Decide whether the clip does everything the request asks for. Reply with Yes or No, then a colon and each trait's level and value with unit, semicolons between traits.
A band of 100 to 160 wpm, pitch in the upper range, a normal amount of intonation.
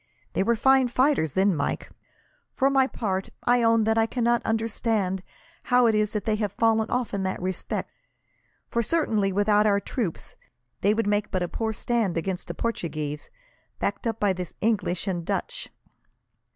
No: average, 170 wpm; high, 215 Hz; average, 3.4 semitones